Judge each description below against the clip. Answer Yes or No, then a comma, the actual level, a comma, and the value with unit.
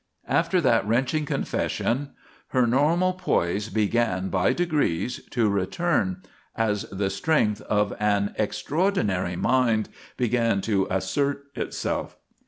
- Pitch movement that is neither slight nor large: No, wide, 6.0 semitones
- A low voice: Yes, low, 115 Hz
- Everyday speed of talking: No, slow, 110 wpm